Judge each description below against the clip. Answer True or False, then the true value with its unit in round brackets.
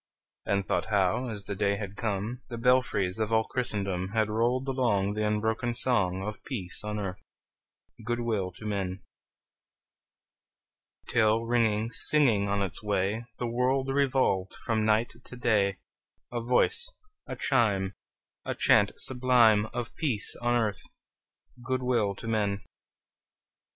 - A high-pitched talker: False (110 Hz)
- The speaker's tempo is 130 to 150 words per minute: True (140 wpm)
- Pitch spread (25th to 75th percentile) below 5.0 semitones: True (3.2 semitones)